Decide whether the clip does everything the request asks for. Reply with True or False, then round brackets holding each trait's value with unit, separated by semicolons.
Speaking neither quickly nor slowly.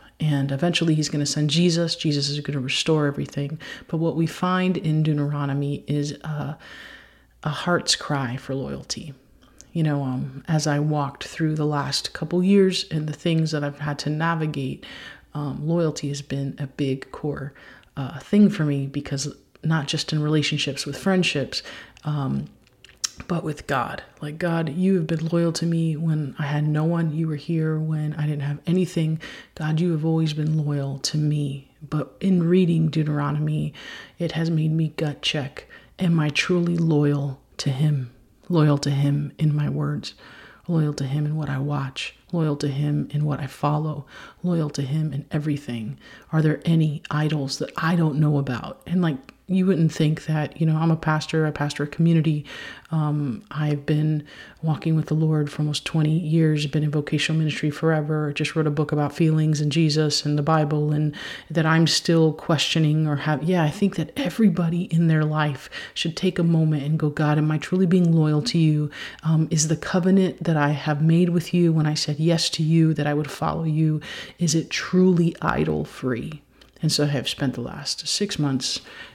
True (190 wpm)